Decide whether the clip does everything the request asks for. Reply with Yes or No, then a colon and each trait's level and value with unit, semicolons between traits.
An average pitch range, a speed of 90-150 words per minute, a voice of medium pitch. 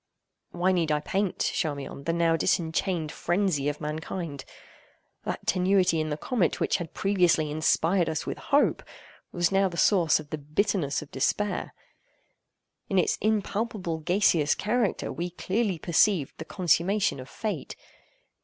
Yes: average, 4.0 semitones; average, 145 wpm; medium, 175 Hz